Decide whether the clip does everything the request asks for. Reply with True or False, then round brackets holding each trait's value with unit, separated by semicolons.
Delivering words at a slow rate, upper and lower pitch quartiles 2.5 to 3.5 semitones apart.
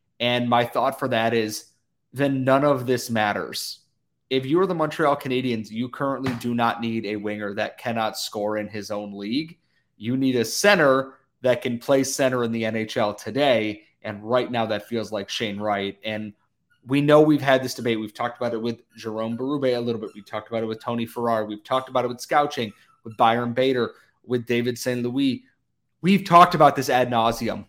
False (205 wpm; 3.2 semitones)